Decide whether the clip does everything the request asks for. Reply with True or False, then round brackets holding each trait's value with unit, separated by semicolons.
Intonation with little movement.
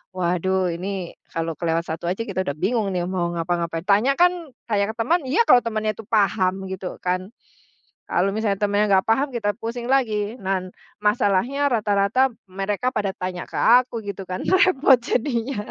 False (4.1 semitones)